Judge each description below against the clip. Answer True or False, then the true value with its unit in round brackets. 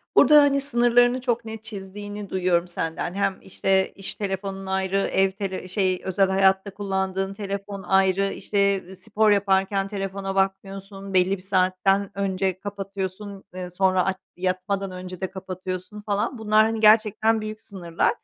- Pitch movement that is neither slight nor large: False (1.5 semitones)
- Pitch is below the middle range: False (195 Hz)